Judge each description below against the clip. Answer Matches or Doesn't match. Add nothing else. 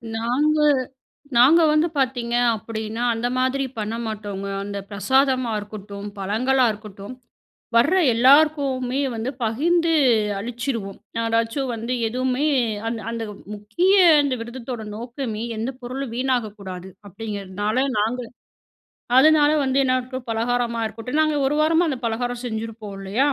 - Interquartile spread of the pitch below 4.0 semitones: Matches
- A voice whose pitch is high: Matches